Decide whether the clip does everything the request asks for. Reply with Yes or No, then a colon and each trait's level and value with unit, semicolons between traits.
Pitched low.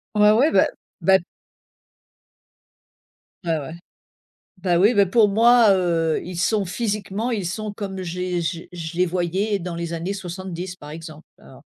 No: medium, 185 Hz